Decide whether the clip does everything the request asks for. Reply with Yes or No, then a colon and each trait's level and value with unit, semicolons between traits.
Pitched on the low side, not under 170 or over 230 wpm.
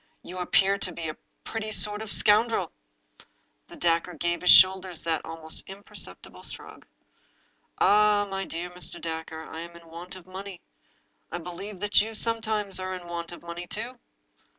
No: medium, 185 Hz; average, 175 wpm